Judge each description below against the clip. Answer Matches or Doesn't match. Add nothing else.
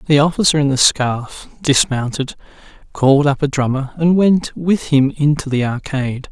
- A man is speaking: Matches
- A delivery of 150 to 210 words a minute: Matches